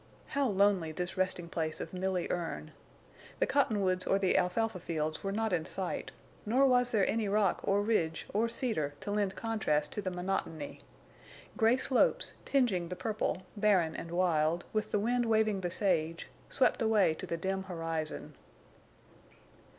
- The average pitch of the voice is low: No, high, 190 Hz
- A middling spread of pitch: Yes, average, 4.4 semitones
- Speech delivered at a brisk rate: No, average, 160 wpm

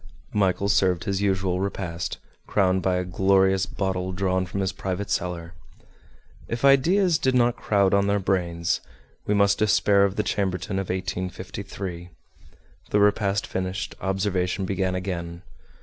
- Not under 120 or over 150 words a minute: Yes, average, 140 wpm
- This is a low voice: Yes, very low, 95 Hz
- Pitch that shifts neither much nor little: No, narrow, 1.5 semitones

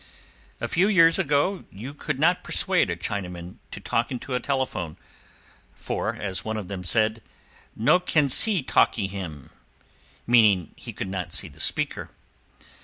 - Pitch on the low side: Yes, low, 115 Hz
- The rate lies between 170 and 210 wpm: No, average, 155 wpm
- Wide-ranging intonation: Yes, wide, 7.9 semitones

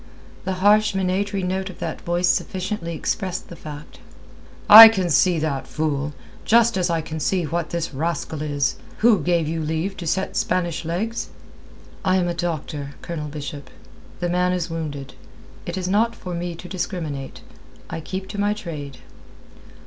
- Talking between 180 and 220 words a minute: No, average, 165 wpm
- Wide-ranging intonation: No, average, 3.3 semitones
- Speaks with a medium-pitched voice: Yes, medium, 175 Hz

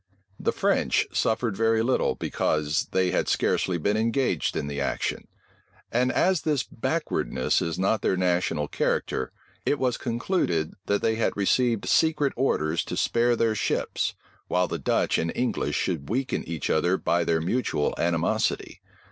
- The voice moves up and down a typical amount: No, wide, 6.6 semitones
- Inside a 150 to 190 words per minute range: Yes, average, 155 wpm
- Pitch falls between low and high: No, low, 100 Hz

